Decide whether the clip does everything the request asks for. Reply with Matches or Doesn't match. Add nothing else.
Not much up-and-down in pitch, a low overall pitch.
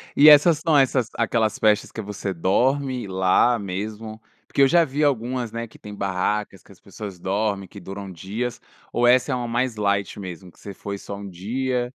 Doesn't match